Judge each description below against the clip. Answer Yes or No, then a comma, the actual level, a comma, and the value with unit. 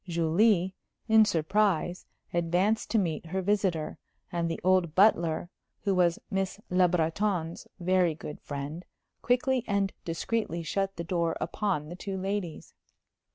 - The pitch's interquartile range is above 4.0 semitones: No, average, 3.1 semitones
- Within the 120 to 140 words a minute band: Yes, slow, 135 wpm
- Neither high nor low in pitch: Yes, medium, 180 Hz